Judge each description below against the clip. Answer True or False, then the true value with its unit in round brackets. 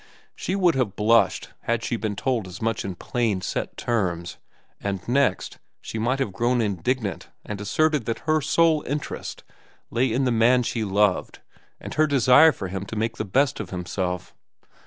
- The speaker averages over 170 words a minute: True (180 wpm)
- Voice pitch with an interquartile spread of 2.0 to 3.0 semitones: False (4.7 semitones)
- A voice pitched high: False (115 Hz)